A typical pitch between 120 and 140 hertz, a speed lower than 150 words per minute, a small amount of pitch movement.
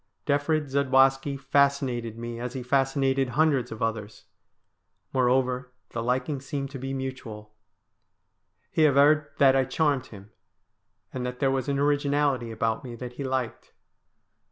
Yes: low, 135 Hz; average, 140 wpm; narrow, 2.2 semitones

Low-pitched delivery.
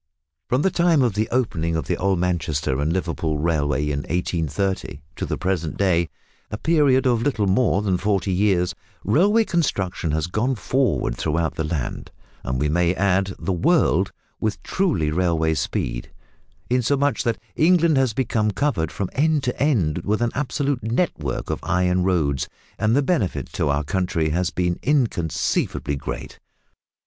Yes: very low, 95 Hz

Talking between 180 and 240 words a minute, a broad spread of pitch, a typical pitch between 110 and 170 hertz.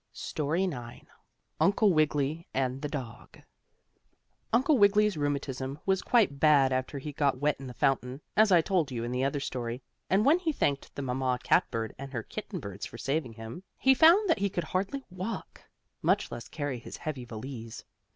Yes: average, 185 wpm; wide, 6.7 semitones; medium, 140 Hz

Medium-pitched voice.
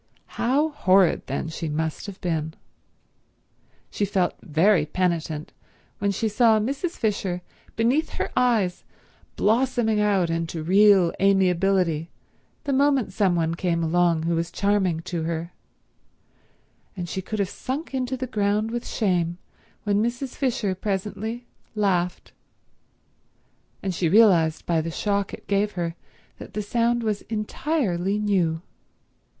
No: high, 195 Hz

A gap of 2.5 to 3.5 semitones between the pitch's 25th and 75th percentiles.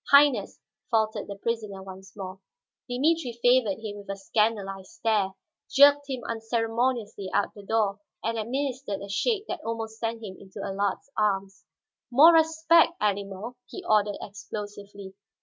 No: average, 3.9 semitones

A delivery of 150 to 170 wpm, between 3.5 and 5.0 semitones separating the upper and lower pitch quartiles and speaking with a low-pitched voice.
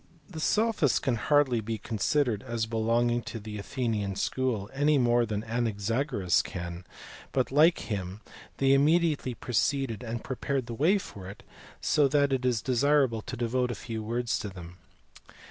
Yes: average, 160 wpm; average, 3.9 semitones; low, 120 Hz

